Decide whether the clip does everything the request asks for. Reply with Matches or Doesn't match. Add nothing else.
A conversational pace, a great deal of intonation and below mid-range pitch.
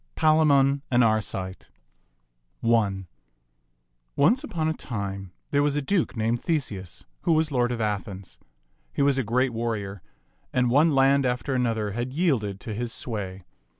Matches